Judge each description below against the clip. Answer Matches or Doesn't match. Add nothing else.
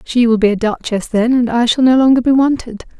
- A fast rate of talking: Matches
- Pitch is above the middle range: Matches